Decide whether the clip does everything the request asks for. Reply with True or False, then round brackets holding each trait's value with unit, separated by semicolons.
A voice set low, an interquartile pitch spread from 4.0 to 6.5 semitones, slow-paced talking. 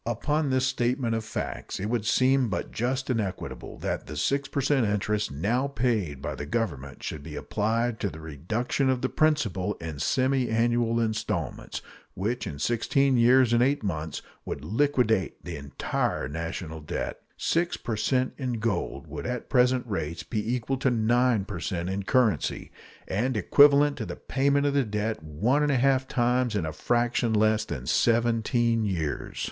False (115 Hz; 4.5 semitones; 175 wpm)